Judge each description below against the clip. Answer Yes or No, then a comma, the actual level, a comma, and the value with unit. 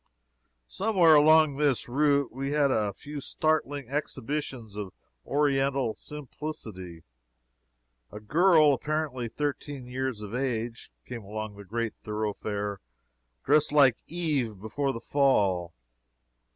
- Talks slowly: Yes, slow, 110 wpm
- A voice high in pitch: No, low, 135 Hz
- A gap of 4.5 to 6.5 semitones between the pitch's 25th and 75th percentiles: Yes, wide, 5.4 semitones